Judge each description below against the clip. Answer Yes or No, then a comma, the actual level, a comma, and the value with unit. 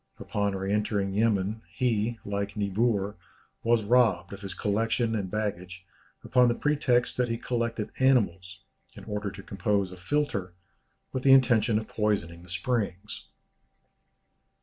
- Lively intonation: No, average, 3.3 semitones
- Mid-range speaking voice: No, low, 105 Hz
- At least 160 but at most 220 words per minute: No, average, 140 wpm